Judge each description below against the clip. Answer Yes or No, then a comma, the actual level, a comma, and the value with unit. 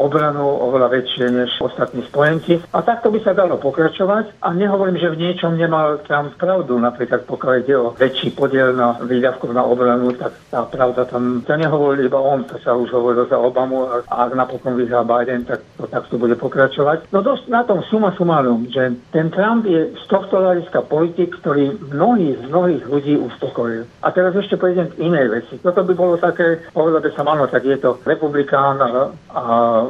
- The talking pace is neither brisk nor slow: No, fast, 190 wpm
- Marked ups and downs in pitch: Yes, wide, 5.8 semitones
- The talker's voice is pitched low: No, medium, 145 Hz